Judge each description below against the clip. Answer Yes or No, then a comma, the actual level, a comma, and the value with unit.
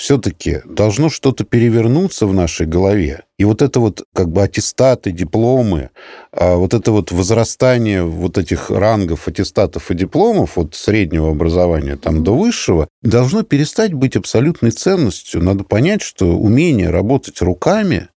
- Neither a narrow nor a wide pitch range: No, wide, 6.1 semitones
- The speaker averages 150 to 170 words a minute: No, average, 140 wpm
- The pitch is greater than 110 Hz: No, low, 105 Hz